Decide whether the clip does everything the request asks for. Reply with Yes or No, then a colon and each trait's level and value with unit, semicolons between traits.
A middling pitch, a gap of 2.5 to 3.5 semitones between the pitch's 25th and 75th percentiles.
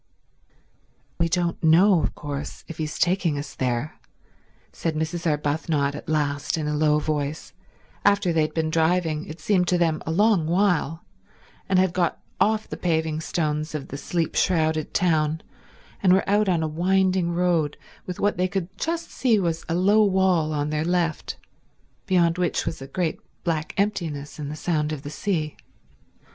Yes: medium, 165 Hz; average, 3.0 semitones